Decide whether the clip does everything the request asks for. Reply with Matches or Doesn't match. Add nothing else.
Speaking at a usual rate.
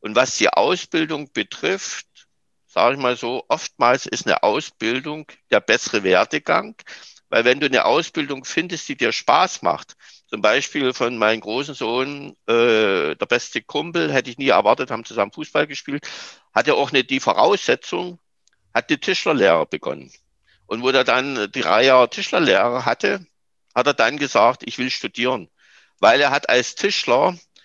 Matches